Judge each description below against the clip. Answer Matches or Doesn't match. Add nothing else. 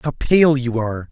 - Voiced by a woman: Doesn't match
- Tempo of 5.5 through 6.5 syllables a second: Matches